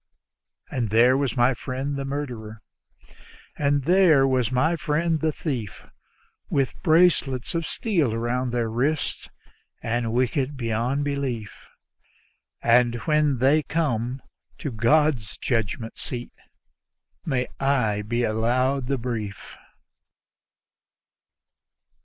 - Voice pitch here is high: No, low, 130 Hz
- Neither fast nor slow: No, slow, 105 wpm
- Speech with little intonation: No, average, 3.6 semitones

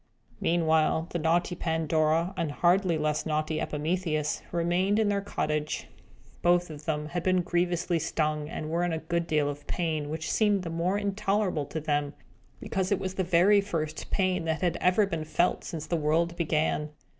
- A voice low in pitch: No, medium, 170 Hz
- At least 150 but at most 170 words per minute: No, average, 180 wpm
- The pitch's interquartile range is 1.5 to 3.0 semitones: Yes, average, 2.7 semitones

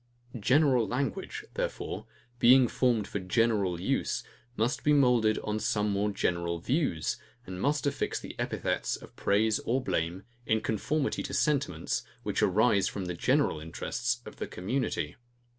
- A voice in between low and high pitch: No, low, 110 Hz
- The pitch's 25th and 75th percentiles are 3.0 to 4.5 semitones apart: No, wide, 5.4 semitones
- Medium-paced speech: Yes, average, 145 wpm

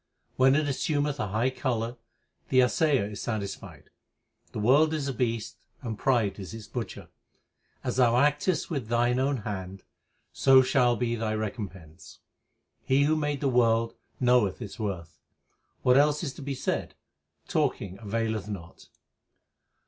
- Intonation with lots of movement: No, average, 4.3 semitones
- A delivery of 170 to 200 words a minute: No, average, 155 wpm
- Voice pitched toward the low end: Yes, low, 120 Hz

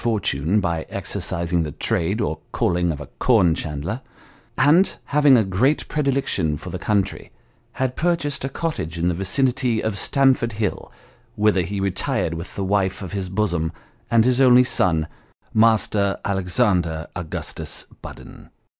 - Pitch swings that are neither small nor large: No, wide, 6.3 semitones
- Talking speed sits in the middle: Yes, average, 150 wpm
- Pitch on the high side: No, low, 100 Hz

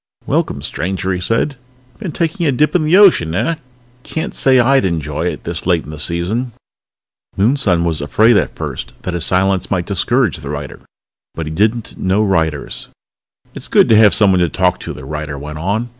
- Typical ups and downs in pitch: No, wide, 6.3 semitones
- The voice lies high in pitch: No, very low, 95 Hz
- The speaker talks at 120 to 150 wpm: No, average, 195 wpm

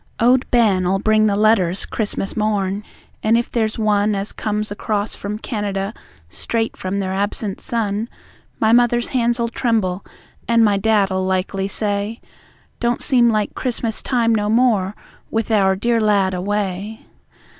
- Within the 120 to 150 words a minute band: Yes, average, 145 wpm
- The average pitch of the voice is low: No, high, 210 Hz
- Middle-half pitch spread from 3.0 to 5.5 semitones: No, narrow, 2.6 semitones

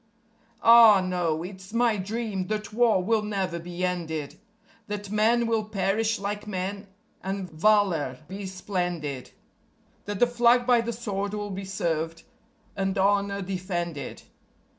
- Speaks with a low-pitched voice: No, high, 195 Hz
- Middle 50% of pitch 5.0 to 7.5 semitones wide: No, average, 2.9 semitones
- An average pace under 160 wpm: Yes, slow, 135 wpm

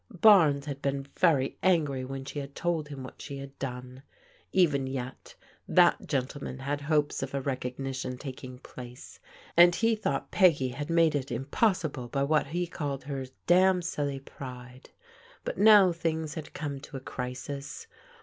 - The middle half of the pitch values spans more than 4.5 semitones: No, average, 3.4 semitones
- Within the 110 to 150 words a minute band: No, average, 160 wpm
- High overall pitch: No, medium, 140 Hz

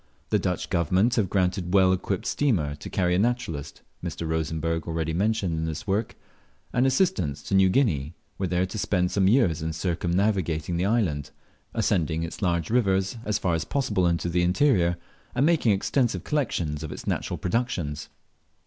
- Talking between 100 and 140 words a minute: No, average, 175 wpm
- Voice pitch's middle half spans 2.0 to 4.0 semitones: No, average, 4.6 semitones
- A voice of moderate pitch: No, very low, 90 Hz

